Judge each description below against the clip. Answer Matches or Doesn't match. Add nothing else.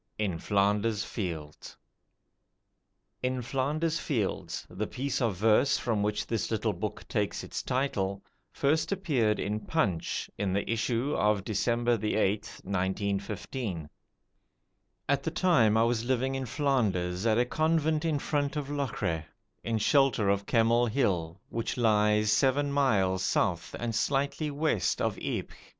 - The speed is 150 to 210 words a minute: Doesn't match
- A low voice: Matches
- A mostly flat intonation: Doesn't match